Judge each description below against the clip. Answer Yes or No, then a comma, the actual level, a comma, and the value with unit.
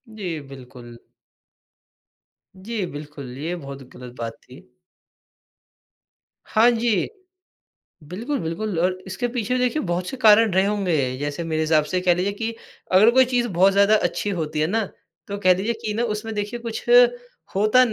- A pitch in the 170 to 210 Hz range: Yes, high, 190 Hz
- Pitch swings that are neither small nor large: No, wide, 6.1 semitones